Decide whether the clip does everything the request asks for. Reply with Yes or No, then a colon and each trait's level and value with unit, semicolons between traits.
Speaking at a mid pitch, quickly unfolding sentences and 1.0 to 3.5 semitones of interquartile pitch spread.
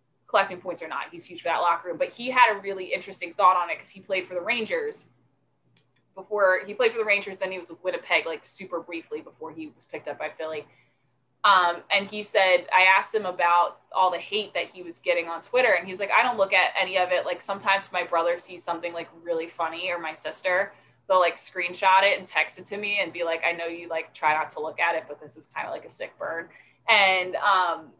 Yes: medium, 180 Hz; fast, 255 wpm; average, 2.8 semitones